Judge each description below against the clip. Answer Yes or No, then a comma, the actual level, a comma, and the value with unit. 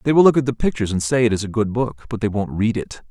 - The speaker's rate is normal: No, fast, 350 wpm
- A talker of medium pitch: No, low, 115 Hz